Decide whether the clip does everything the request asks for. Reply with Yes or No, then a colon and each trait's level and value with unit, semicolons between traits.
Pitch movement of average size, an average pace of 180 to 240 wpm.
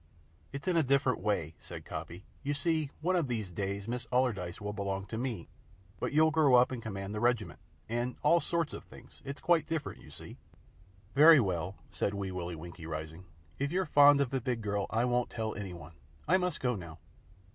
No: wide, 6.5 semitones; fast, 205 wpm